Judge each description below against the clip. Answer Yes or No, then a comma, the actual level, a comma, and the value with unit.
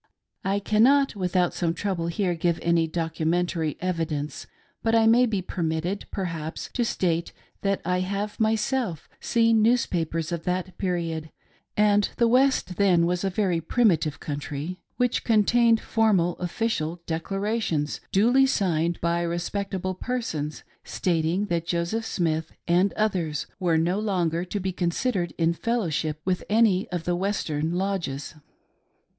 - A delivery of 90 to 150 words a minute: Yes, average, 140 wpm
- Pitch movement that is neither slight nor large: Yes, average, 4.0 semitones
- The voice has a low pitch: No, medium, 180 Hz